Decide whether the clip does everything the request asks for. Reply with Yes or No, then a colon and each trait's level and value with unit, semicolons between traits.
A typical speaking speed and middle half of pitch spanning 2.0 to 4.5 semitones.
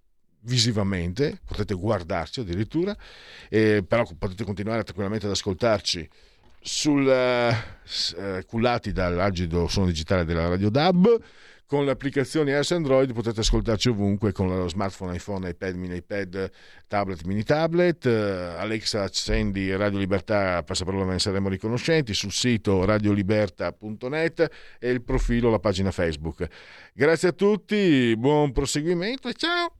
No: average, 125 wpm; average, 5.3 semitones